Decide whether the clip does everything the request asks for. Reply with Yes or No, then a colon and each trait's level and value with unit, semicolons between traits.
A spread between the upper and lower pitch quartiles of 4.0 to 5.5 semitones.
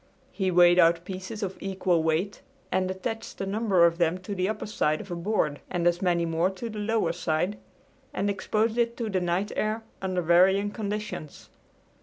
No: average, 3.3 semitones